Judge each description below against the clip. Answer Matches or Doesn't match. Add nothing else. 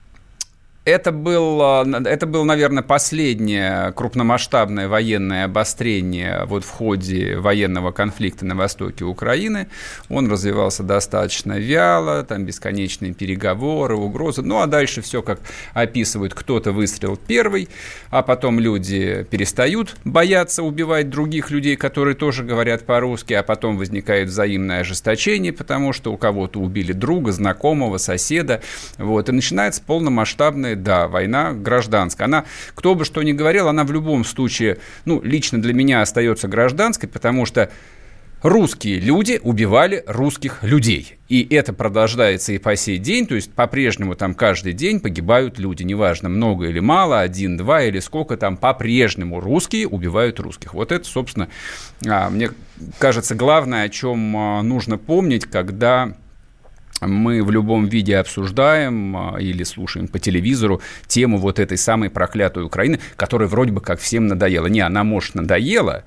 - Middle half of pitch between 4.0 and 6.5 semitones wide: Matches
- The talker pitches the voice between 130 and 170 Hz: Doesn't match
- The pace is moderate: Matches